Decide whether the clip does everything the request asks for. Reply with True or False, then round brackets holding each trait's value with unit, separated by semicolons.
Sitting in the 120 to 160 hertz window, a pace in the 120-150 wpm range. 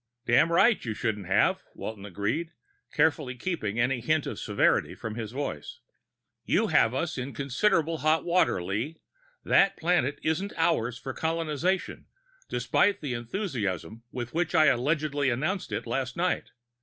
True (140 Hz; 145 wpm)